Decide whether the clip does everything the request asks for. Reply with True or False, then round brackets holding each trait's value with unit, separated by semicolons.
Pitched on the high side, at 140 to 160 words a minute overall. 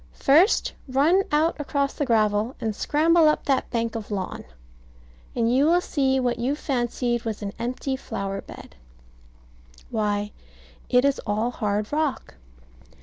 True (250 Hz; 145 wpm)